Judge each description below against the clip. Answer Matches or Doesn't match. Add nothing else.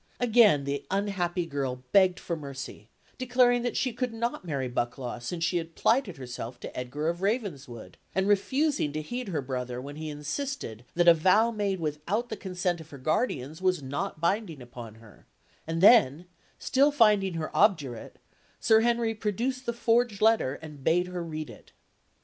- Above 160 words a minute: Matches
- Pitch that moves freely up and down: Matches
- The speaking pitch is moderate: Matches